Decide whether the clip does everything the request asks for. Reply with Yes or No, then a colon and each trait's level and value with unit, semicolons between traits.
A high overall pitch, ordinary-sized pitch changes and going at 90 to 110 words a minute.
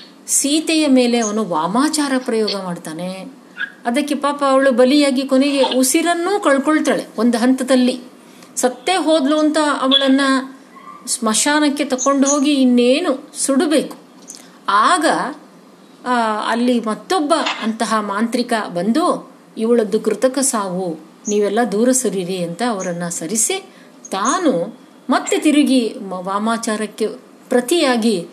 Yes: very high, 255 Hz; average, 4.3 semitones; average, 95 wpm